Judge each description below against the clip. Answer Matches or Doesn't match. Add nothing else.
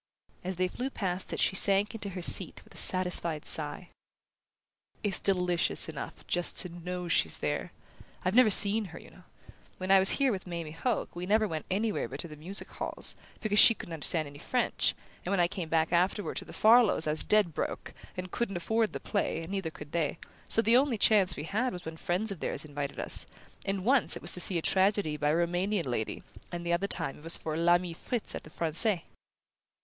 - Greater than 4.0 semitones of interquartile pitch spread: Doesn't match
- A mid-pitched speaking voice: Matches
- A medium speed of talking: Doesn't match